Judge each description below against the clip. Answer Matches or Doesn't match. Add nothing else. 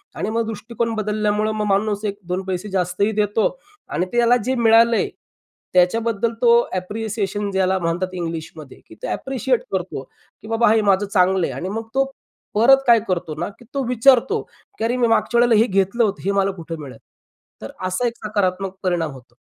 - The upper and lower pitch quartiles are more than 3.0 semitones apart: Matches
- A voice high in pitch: Matches